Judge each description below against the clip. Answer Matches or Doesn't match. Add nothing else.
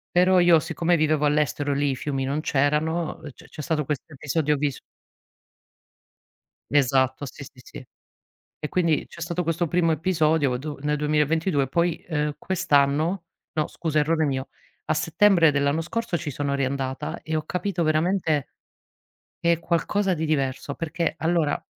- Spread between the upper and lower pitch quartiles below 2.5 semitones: Doesn't match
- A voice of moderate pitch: Matches